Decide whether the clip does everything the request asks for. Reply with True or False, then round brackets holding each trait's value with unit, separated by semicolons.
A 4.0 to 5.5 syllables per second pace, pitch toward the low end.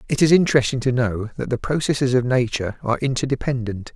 False (6.6 syllables/s; 125 Hz)